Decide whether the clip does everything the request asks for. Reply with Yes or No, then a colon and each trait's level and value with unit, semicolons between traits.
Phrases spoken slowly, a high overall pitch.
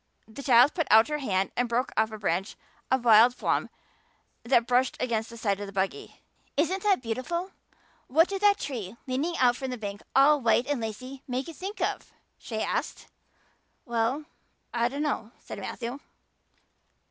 No: average, 175 wpm; very high, 250 Hz